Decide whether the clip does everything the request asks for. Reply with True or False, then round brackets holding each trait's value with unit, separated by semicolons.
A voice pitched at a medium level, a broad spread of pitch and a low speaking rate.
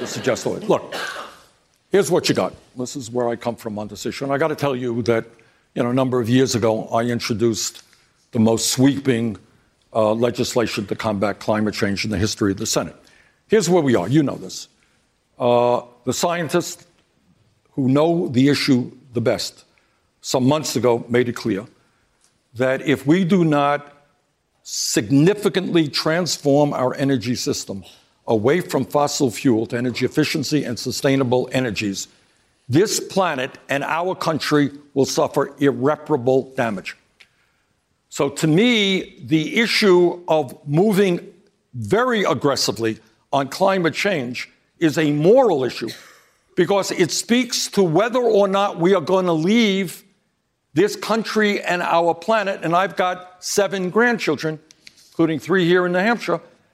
False (145 Hz; 6.5 semitones; 150 wpm)